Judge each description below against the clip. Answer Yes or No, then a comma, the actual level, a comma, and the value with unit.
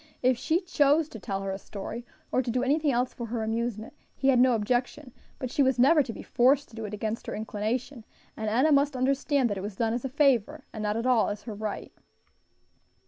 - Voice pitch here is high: Yes, high, 245 Hz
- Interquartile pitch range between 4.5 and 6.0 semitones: No, average, 3.7 semitones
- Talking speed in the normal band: No, fast, 235 wpm